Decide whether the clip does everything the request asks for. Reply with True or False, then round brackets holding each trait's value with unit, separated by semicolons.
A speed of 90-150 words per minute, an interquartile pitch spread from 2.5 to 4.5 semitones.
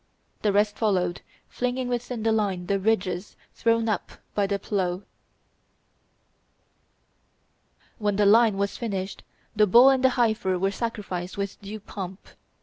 True (140 wpm; 2.8 semitones)